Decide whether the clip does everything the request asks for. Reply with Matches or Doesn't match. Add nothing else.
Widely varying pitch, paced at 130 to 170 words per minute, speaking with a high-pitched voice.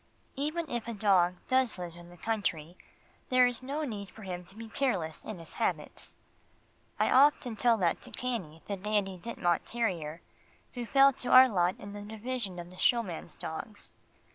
Doesn't match